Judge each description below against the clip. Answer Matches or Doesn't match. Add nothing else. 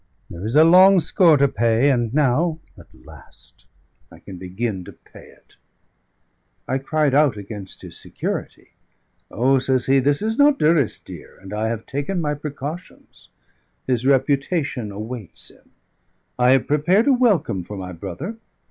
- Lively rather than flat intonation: Matches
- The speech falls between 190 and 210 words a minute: Doesn't match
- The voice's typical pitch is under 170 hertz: Matches